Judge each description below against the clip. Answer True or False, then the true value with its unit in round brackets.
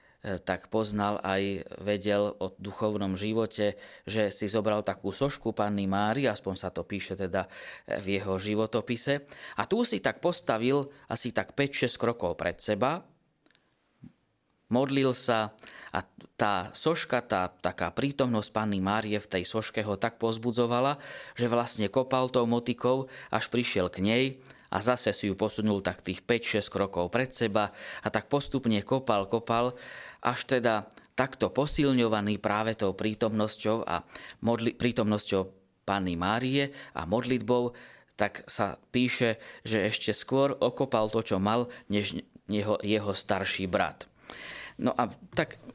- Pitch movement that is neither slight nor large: True (3.3 semitones)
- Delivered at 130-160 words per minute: True (140 wpm)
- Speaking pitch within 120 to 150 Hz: False (110 Hz)